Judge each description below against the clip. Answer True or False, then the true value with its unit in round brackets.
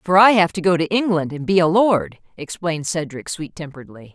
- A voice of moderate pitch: True (170 Hz)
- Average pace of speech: False (215 wpm)